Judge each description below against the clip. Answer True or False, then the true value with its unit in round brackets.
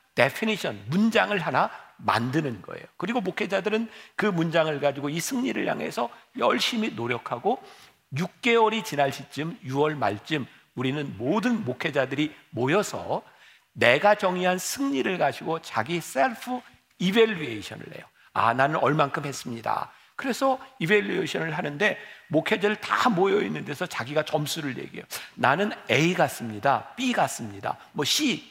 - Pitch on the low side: False (165 Hz)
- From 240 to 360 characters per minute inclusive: True (315 characters per minute)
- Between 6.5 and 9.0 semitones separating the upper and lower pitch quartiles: True (7.1 semitones)